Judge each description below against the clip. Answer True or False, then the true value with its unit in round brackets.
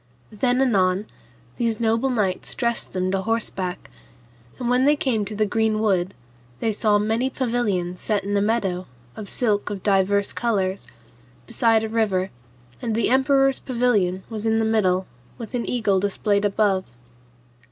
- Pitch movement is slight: False (3.3 semitones)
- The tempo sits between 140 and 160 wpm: True (155 wpm)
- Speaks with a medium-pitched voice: False (215 Hz)